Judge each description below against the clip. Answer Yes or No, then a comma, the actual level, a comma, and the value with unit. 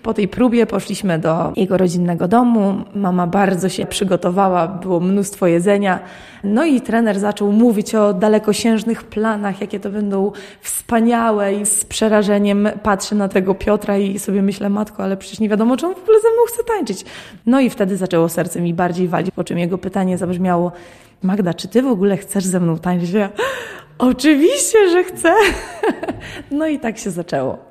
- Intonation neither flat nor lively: Yes, average, 3.1 semitones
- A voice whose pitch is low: No, high, 205 Hz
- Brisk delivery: Yes, fast, 175 wpm